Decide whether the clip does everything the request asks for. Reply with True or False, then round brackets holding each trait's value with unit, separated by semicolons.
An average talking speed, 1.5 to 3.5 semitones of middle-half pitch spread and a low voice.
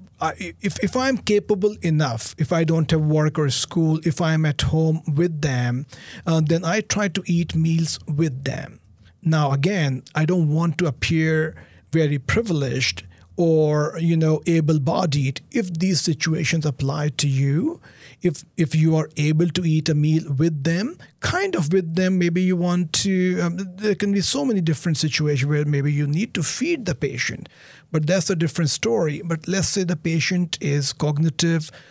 False (180 wpm; 3.0 semitones; 160 Hz)